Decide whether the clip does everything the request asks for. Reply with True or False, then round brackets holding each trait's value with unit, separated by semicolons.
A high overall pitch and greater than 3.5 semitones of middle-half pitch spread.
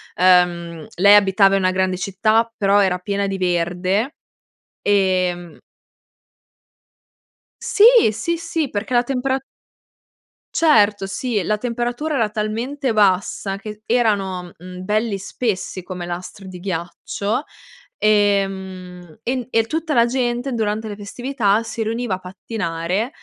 True (205 Hz; 4.0 semitones)